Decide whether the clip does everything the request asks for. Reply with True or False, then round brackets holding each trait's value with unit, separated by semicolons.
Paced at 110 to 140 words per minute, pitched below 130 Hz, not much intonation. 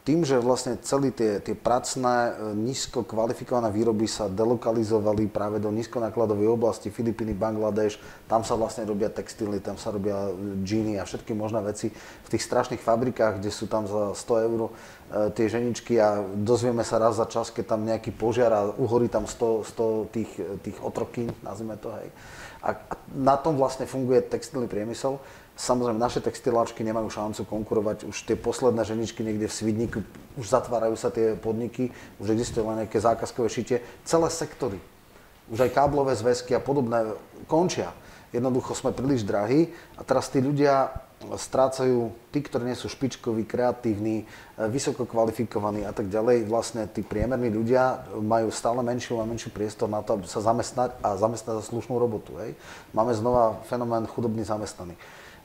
False (160 wpm; 115 Hz; 2.1 semitones)